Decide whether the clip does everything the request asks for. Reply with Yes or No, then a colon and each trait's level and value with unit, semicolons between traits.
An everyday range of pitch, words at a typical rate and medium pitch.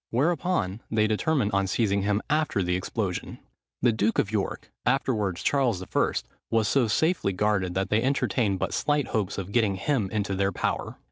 No: average, 4.0 semitones; average, 175 wpm; low, 105 Hz